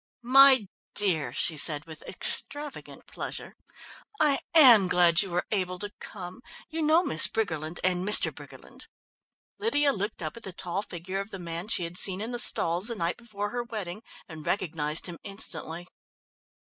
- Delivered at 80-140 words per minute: No, average, 170 wpm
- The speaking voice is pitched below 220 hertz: Yes, high, 190 Hz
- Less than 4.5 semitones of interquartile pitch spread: No, average, 4.8 semitones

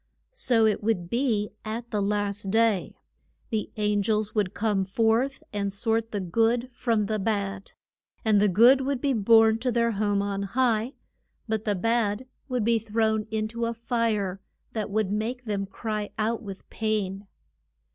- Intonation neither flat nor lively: No, narrow, 2.1 semitones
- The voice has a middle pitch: No, high, 220 Hz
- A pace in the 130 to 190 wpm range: Yes, average, 165 wpm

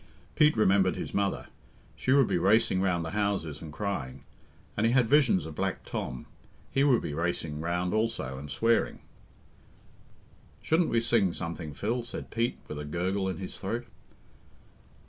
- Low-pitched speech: Yes, very low, 95 Hz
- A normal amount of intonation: No, wide, 5.9 semitones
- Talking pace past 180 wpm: No, average, 165 wpm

